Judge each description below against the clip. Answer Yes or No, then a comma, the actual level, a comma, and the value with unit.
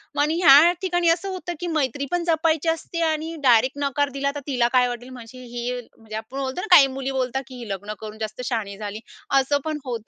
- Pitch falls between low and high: No, very high, 270 Hz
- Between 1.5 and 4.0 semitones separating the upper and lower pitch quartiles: No, average, 5.0 semitones